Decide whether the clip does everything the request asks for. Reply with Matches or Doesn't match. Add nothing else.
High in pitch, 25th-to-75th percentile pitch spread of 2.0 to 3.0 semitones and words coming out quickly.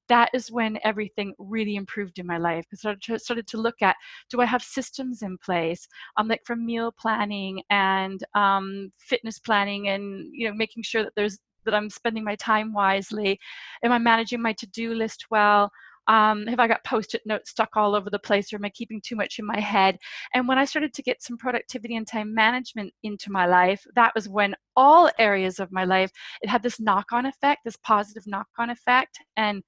Matches